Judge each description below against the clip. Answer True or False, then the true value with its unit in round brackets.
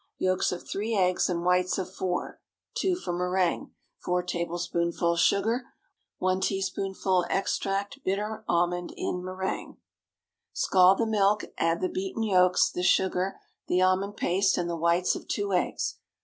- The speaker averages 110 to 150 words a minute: True (140 wpm)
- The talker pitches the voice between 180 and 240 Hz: True (185 Hz)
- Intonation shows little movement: True (1.7 semitones)